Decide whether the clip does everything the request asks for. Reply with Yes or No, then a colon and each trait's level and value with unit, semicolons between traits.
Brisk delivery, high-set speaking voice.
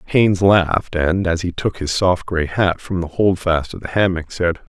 No: fast, 215 wpm; very low, 90 Hz